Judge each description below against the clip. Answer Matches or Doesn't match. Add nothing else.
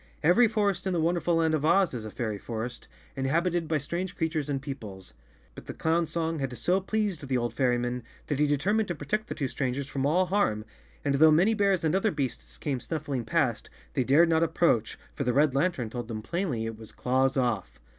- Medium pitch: Matches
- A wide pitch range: Matches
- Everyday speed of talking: Doesn't match